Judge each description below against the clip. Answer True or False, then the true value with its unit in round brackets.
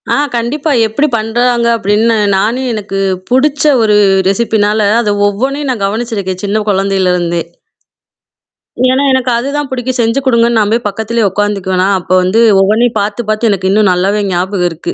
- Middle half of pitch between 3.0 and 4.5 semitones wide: True (3.4 semitones)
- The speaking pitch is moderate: False (215 Hz)